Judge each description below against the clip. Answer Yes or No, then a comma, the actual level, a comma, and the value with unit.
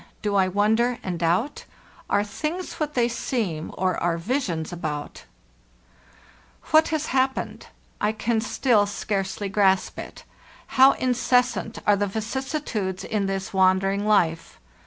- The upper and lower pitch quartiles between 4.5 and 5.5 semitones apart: Yes, average, 4.8 semitones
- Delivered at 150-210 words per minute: No, slow, 135 wpm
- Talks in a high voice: Yes, high, 210 Hz